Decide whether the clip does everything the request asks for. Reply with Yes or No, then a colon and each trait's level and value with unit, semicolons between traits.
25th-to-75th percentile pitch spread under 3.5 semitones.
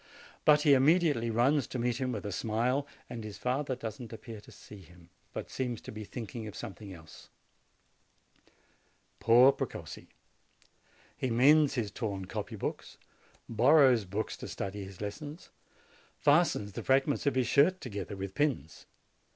No: average, 4.8 semitones